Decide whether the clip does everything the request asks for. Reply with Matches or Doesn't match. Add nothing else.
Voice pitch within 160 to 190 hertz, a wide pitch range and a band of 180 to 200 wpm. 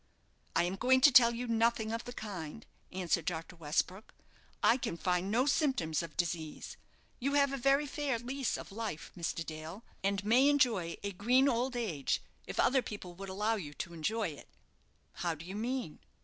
Doesn't match